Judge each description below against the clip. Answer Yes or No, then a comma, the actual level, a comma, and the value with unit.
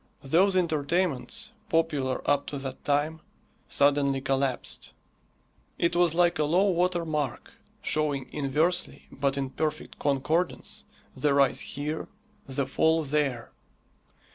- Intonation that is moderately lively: Yes, average, 3.4 semitones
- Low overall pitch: No, medium, 150 Hz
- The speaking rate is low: Yes, slow, 115 wpm